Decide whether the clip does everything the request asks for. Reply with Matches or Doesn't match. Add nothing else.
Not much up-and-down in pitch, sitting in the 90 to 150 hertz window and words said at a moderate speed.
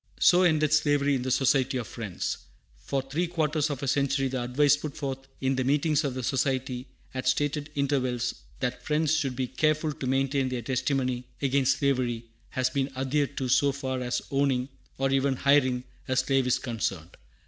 Matches